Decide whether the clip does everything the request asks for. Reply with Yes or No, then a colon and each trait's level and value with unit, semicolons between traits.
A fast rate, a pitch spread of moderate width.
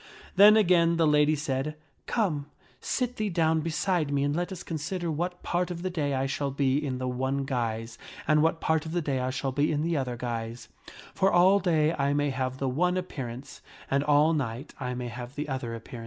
Yes: fast, 210 wpm; average, 4.3 semitones